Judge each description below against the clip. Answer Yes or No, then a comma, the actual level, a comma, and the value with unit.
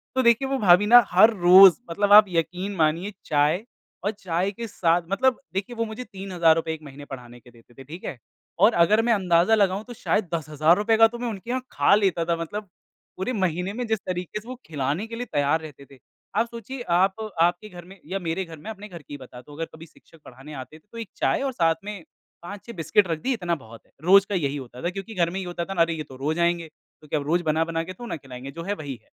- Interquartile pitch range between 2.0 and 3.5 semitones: No, average, 4.7 semitones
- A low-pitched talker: No, medium, 175 Hz